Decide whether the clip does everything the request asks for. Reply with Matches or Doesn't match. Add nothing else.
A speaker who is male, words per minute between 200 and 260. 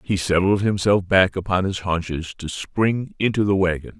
Doesn't match